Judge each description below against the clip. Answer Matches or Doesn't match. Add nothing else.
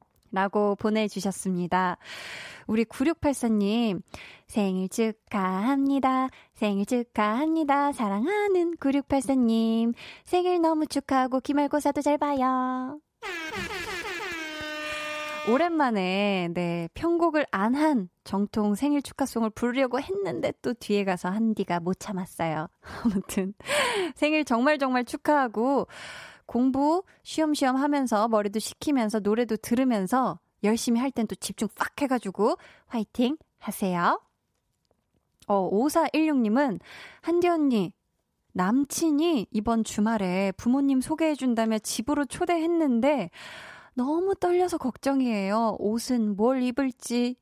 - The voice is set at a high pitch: Matches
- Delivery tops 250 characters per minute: Doesn't match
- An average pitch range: Doesn't match